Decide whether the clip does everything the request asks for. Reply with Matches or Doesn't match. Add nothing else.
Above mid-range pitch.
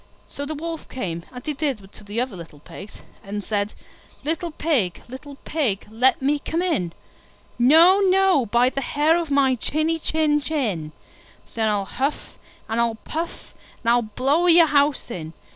Matches